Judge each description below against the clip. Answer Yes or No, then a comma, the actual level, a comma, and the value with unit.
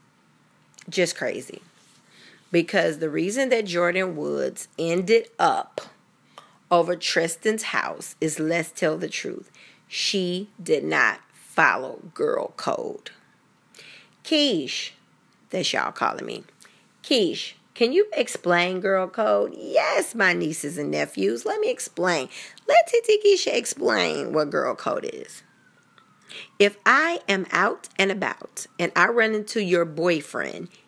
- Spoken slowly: Yes, slow, 120 wpm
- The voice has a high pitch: Yes, high, 195 Hz